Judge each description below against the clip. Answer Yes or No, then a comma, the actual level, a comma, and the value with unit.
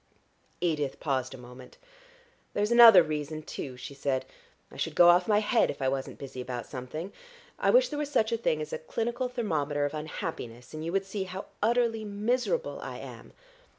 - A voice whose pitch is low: No, medium, 165 Hz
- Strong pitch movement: Yes, wide, 8.2 semitones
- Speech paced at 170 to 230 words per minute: Yes, average, 190 wpm